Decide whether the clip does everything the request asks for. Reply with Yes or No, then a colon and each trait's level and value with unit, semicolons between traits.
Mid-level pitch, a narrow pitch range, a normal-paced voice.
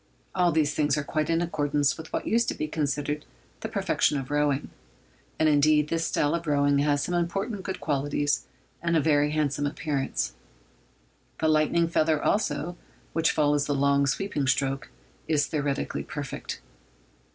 Yes: medium, 150 Hz; narrow, 2.1 semitones; average, 160 wpm